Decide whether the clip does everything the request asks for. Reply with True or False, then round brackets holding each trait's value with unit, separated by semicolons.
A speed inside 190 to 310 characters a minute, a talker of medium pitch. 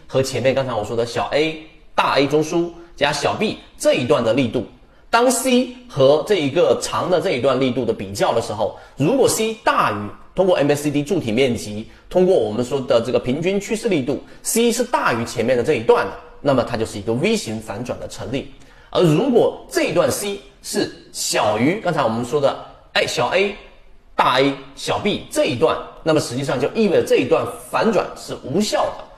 True (290 characters per minute; 155 Hz)